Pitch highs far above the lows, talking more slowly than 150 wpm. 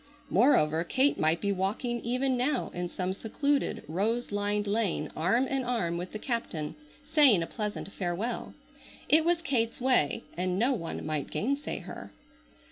No: wide, 6.1 semitones; average, 155 wpm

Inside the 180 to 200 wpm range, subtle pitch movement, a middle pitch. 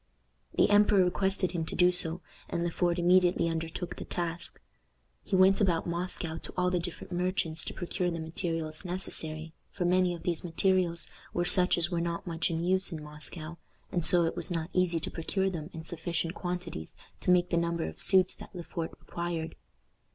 Yes: average, 195 wpm; narrow, 1.6 semitones; medium, 175 Hz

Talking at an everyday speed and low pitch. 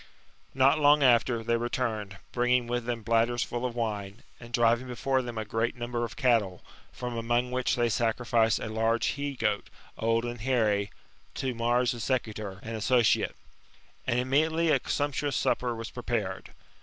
Yes: average, 165 wpm; low, 120 Hz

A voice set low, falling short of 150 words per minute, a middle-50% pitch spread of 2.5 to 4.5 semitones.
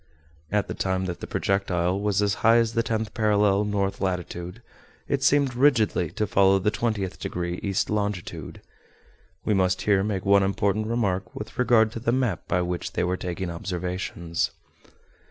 No: low, 100 Hz; average, 170 wpm; average, 2.9 semitones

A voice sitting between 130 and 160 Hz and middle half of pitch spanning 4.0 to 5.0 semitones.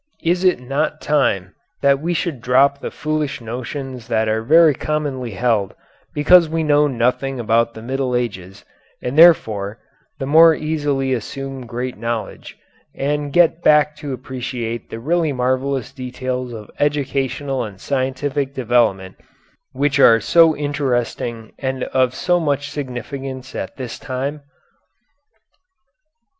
No: low, 135 Hz; average, 3.3 semitones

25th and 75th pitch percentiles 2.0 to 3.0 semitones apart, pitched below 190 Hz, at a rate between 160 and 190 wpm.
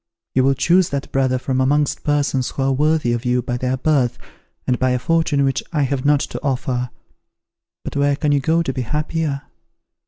No: narrow, 2.4 semitones; low, 135 Hz; fast, 205 wpm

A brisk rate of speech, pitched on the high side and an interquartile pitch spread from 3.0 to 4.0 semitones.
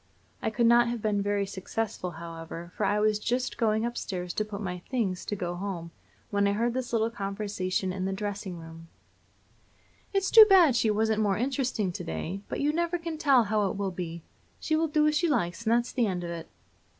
No: fast, 220 wpm; high, 210 Hz; average, 4.5 semitones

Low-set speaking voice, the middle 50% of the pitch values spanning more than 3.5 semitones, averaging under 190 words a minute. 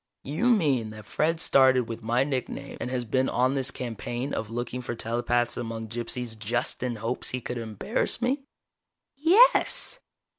No: low, 125 Hz; average, 3.0 semitones; average, 160 wpm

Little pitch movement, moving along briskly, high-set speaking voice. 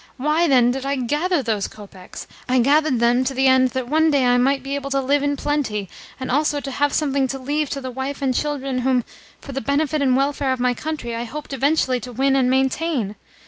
Yes: narrow, 2.3 semitones; fast, 230 wpm; very high, 270 Hz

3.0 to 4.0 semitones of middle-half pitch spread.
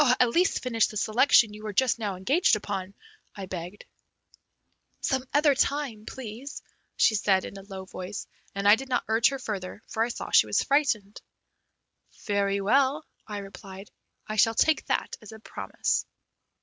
No: average, 4.6 semitones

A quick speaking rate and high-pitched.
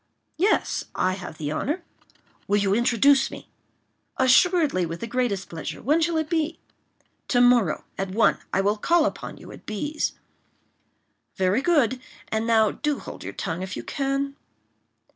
No: average, 160 wpm; high, 245 Hz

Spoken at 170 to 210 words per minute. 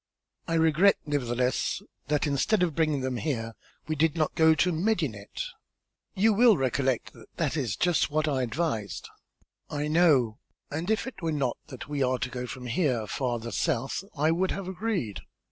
Yes: average, 175 wpm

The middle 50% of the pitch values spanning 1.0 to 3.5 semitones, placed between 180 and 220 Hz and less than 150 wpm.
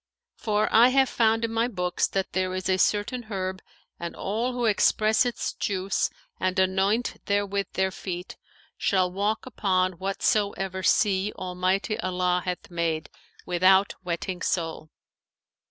Yes: narrow, 2.6 semitones; high, 190 Hz; average, 140 wpm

